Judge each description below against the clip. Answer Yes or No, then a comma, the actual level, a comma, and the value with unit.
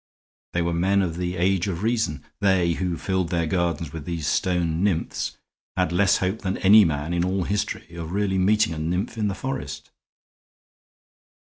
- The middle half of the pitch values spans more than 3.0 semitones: No, average, 2.7 semitones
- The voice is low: Yes, very low, 90 Hz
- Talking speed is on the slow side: No, average, 175 wpm